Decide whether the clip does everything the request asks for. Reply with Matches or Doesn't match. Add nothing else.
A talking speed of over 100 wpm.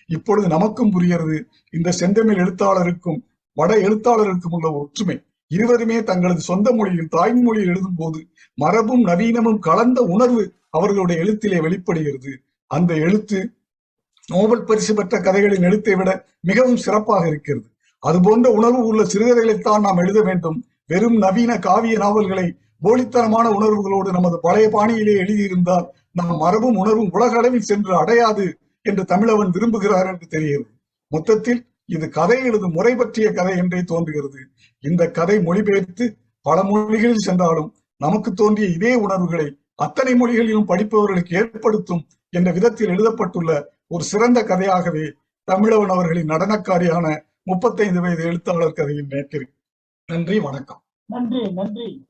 Matches